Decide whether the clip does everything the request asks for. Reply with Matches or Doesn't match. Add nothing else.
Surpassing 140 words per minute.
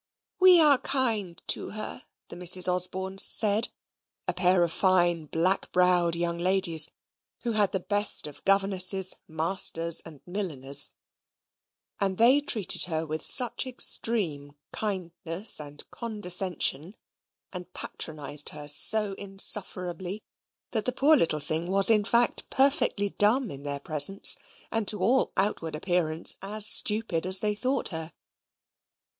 Doesn't match